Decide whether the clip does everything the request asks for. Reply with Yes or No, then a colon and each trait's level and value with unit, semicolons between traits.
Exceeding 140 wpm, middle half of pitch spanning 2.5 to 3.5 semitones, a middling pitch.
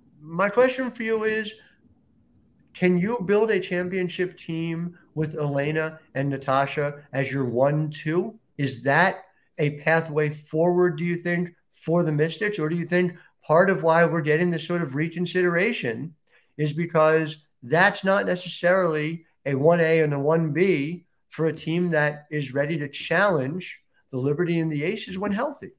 Yes: average, 160 wpm; average, 2.9 semitones; medium, 165 Hz